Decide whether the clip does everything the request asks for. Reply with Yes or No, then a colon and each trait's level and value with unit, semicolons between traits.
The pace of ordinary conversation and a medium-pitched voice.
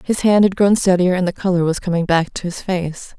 No: fast, 265 wpm; medium, 180 Hz